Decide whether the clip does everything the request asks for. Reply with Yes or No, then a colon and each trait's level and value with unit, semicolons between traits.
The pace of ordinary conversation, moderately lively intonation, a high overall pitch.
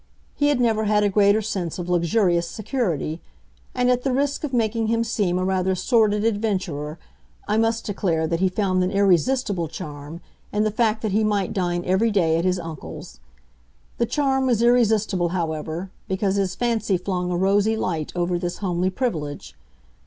Yes: average, 175 wpm; average, 4.2 semitones; high, 195 Hz